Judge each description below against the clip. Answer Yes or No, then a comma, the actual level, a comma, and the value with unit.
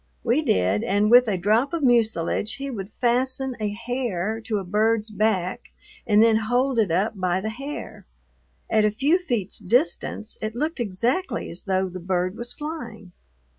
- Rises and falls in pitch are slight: No, average, 4.2 semitones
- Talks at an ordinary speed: Yes, average, 170 wpm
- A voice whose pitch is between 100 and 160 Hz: No, high, 220 Hz